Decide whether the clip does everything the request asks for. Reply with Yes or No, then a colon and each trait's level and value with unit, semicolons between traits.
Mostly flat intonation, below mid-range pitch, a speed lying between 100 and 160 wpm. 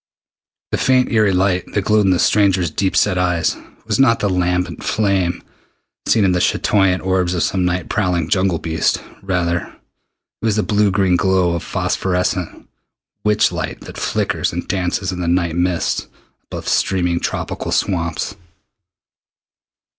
Yes: narrow, 2.0 semitones; very low, 90 Hz; average, 155 wpm